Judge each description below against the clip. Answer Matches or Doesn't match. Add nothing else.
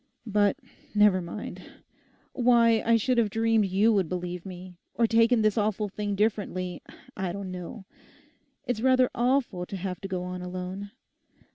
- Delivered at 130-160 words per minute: Matches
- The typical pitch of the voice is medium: Doesn't match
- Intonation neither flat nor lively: Matches